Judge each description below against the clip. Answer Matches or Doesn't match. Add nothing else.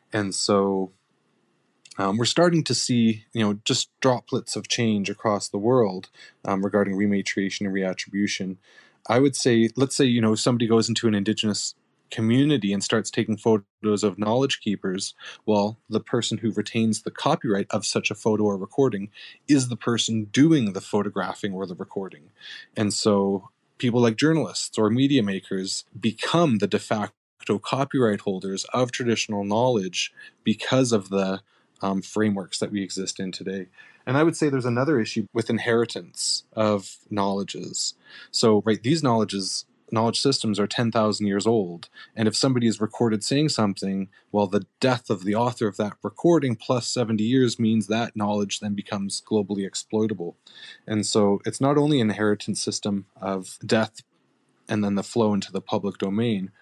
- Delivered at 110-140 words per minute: Doesn't match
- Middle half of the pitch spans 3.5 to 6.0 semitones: Doesn't match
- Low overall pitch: Matches